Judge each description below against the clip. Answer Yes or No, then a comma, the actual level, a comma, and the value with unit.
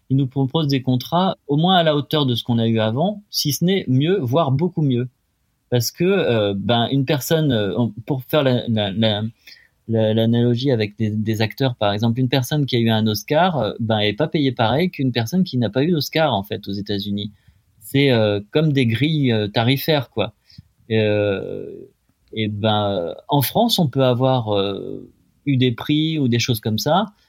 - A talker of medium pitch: No, low, 125 Hz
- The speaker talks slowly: No, average, 200 wpm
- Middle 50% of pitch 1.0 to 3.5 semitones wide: No, average, 5.0 semitones